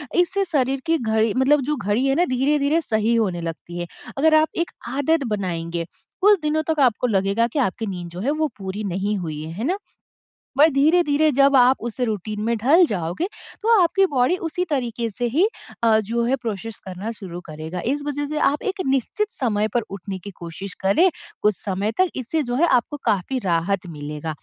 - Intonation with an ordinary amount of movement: No, wide, 7.3 semitones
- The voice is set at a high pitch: Yes, high, 235 Hz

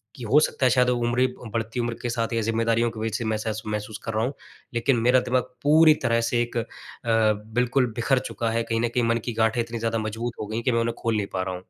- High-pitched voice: No, low, 115 Hz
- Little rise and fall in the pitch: Yes, narrow, 1.4 semitones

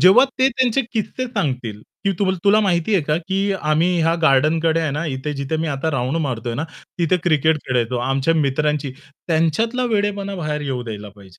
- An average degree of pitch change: No, wide, 5.8 semitones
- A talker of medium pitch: Yes, medium, 160 Hz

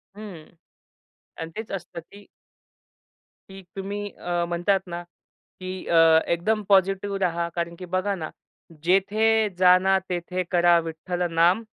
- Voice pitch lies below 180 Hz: No, medium, 185 Hz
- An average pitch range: No, narrow, 2.3 semitones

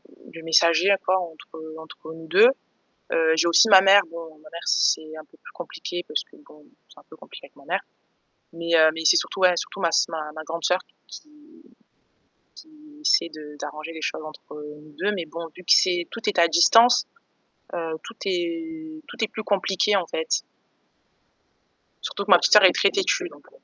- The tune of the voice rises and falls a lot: Yes, wide, 6.0 semitones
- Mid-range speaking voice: Yes, medium, 175 Hz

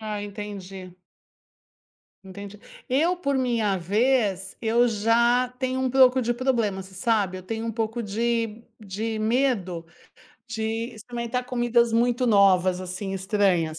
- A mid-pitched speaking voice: No, high, 220 Hz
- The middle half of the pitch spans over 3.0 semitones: Yes, average, 3.6 semitones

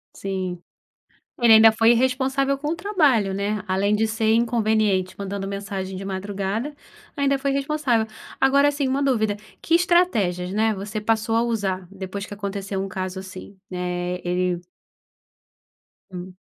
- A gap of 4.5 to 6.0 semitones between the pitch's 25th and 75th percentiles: Yes, average, 4.9 semitones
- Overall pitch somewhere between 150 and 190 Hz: No, high, 210 Hz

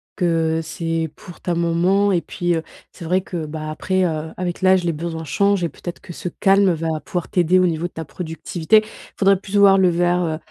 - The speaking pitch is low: No, medium, 175 Hz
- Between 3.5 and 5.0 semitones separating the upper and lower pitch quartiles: No, narrow, 2.4 semitones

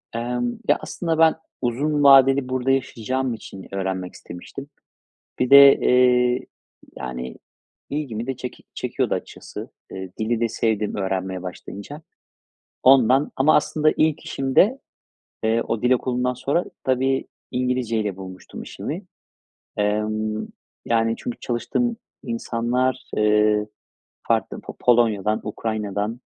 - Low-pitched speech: Yes, low, 120 Hz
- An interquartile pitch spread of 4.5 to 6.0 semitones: No, average, 3.8 semitones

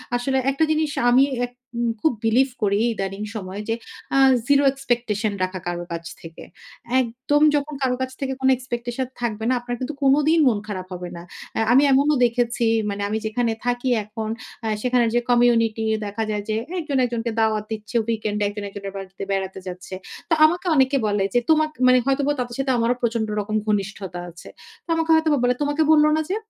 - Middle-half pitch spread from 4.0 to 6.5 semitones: Yes, average, 4.4 semitones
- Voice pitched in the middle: No, high, 235 Hz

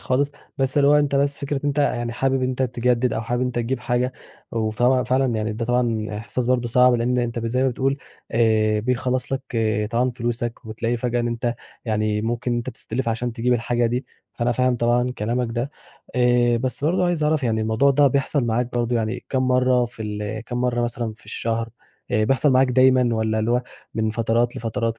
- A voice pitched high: No, low, 120 Hz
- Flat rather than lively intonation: Yes, narrow, 1.8 semitones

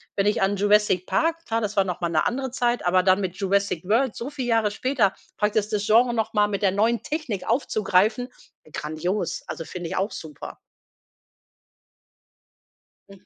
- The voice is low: No, high, 205 Hz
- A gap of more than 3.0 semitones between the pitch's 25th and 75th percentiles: Yes, average, 3.8 semitones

